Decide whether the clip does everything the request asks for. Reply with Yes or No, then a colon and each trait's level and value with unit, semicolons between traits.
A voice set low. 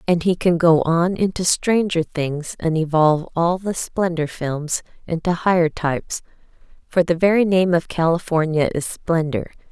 No: medium, 170 Hz